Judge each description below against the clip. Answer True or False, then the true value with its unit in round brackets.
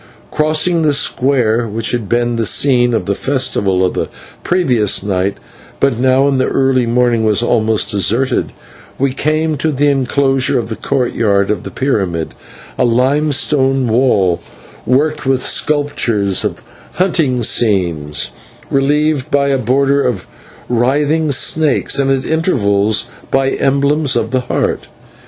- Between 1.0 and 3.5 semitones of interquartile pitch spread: False (4.0 semitones)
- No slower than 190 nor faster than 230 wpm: False (140 wpm)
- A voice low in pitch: True (130 Hz)